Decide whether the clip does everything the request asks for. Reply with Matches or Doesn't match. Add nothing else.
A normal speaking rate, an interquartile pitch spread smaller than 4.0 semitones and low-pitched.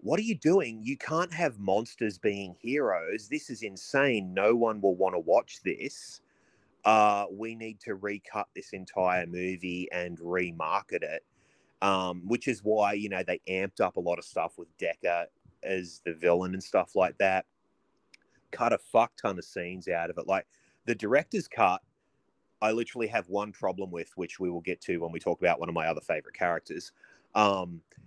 Matches